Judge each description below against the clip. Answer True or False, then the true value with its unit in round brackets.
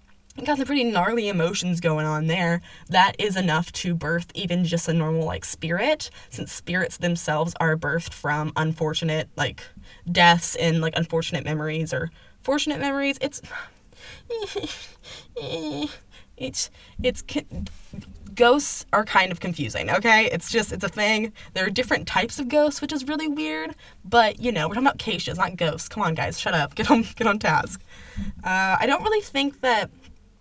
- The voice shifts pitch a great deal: True (7.6 semitones)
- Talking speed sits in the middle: True (170 wpm)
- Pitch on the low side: False (180 Hz)